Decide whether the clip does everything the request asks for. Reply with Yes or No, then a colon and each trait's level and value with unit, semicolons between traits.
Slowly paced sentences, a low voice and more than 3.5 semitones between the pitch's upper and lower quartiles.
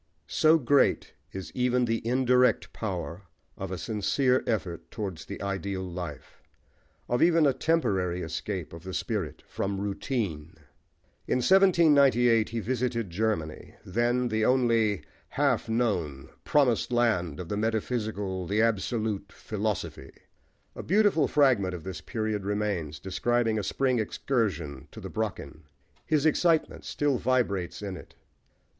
Yes: slow, 130 wpm; low, 110 Hz; average, 5.1 semitones